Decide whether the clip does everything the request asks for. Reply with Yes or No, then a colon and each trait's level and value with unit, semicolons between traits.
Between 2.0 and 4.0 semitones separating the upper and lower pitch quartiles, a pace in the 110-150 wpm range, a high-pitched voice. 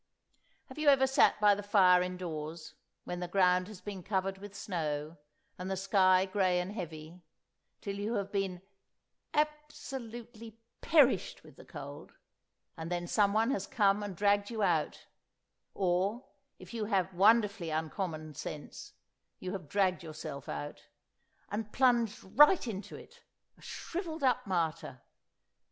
Yes: average, 3.7 semitones; average, 140 wpm; high, 195 Hz